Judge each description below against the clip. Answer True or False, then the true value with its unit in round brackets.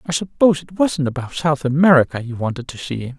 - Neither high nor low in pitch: True (145 Hz)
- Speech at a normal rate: False (225 wpm)